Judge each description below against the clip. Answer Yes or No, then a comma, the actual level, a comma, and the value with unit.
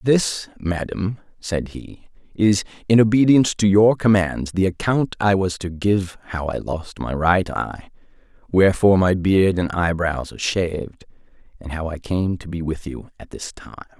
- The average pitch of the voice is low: Yes, very low, 95 Hz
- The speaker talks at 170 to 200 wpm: Yes, average, 175 wpm